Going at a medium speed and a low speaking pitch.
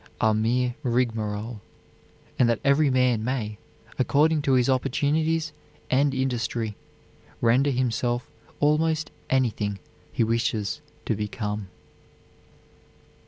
No: slow, 100 wpm; low, 125 Hz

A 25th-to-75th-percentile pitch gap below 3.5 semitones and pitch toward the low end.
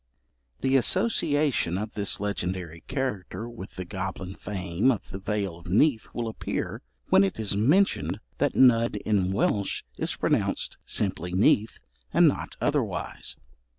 No: average, 4.1 semitones; low, 100 Hz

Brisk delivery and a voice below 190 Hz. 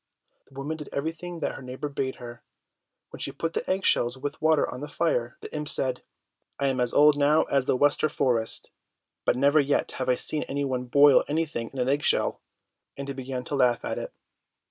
Yes: fast, 215 wpm; medium, 140 Hz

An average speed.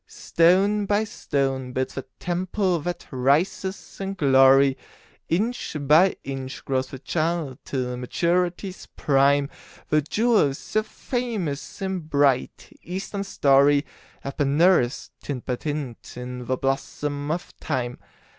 No: slow, 125 wpm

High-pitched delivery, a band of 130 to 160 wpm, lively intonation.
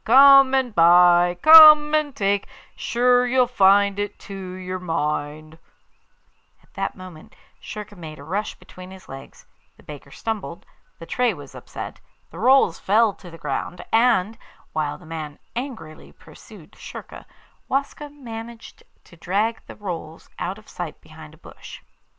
Yes: high, 195 Hz; average, 150 wpm; wide, 6.4 semitones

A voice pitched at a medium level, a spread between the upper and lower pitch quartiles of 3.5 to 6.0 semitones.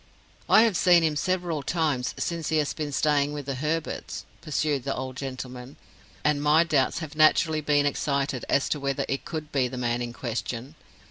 No: medium, 145 Hz; average, 2.9 semitones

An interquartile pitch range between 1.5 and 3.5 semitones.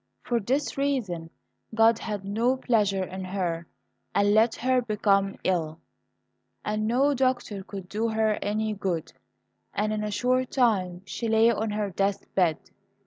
Yes: average, 3.1 semitones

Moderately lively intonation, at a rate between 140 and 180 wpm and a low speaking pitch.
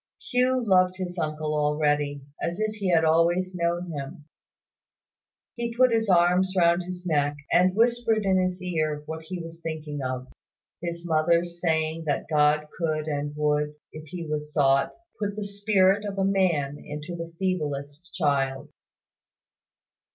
No: average, 3.7 semitones; average, 150 wpm; medium, 170 Hz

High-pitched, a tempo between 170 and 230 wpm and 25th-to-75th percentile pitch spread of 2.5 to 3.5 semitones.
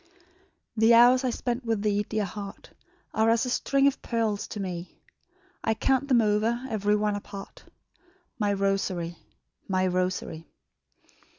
No: high, 210 Hz; average, 140 wpm; average, 3.0 semitones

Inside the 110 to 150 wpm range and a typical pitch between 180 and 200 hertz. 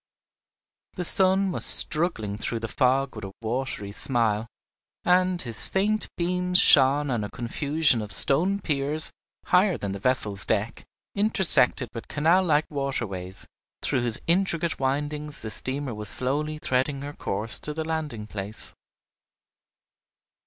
No: average, 140 wpm; medium, 140 Hz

